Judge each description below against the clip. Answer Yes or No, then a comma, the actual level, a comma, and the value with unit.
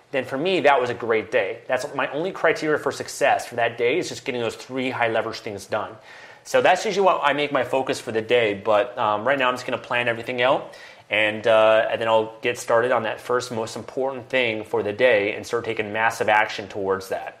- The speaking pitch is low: Yes, low, 120 Hz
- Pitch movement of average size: Yes, average, 3.3 semitones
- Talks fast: Yes, fast, 240 wpm